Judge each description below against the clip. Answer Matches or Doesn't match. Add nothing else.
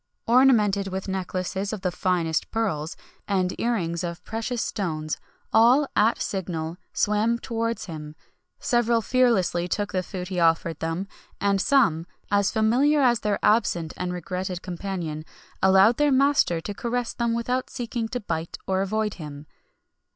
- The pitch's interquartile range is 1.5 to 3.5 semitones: Doesn't match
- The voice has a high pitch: Matches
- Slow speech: Doesn't match